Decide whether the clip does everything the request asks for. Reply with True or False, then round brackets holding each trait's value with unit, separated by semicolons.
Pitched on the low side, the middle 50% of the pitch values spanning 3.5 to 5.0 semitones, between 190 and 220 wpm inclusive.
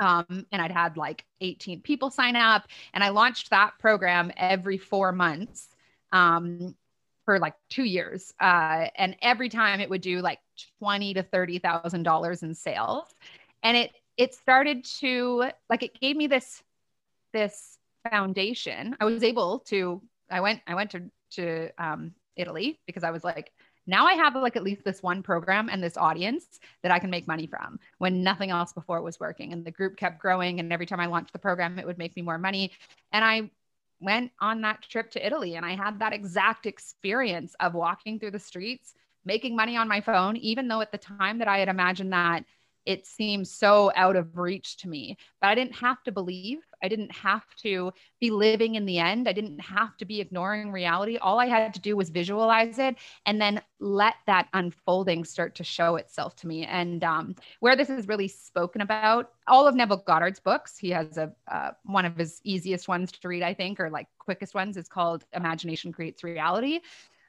False (195 Hz; 3.9 semitones; 200 wpm)